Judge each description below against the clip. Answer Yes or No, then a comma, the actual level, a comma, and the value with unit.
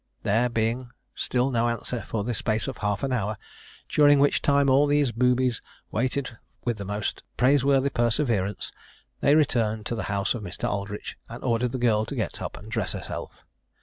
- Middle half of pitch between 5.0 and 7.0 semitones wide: No, average, 3.5 semitones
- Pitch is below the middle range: Yes, low, 120 Hz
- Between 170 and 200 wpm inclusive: Yes, average, 180 wpm